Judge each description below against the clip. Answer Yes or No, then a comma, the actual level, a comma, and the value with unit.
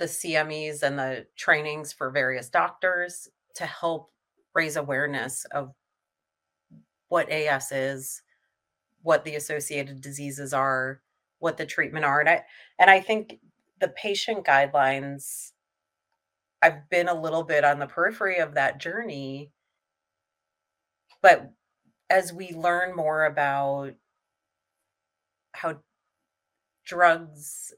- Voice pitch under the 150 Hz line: Yes, medium, 140 Hz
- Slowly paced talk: Yes, slow, 110 wpm